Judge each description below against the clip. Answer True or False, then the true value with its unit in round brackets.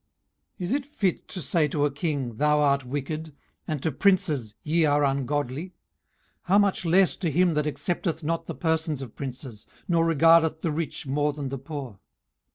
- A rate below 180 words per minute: False (185 wpm)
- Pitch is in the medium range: True (150 Hz)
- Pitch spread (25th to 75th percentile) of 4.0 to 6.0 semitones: False (3.1 semitones)